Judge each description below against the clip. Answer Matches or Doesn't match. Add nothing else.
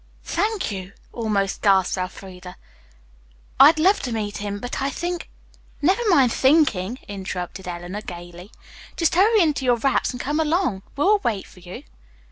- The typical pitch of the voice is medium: Doesn't match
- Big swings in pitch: Matches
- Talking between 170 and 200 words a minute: Doesn't match